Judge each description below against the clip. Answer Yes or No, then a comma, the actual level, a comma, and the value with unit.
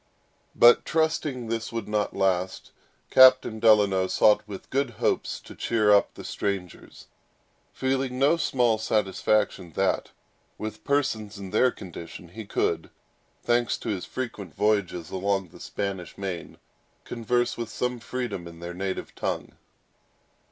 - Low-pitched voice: Yes, low, 105 Hz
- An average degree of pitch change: Yes, average, 4.1 semitones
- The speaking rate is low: Yes, slow, 130 wpm